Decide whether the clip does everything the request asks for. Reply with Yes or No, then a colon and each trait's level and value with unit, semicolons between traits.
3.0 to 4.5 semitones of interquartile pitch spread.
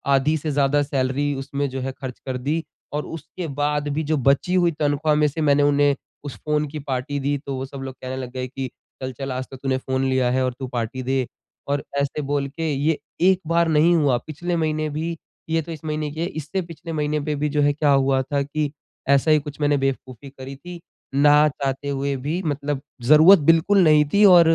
No: narrow, 2.4 semitones